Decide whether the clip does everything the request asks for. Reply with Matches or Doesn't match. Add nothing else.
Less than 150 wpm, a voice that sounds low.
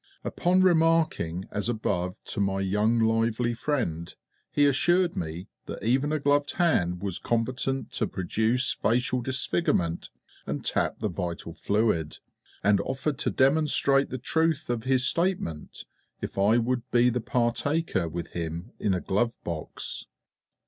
Matches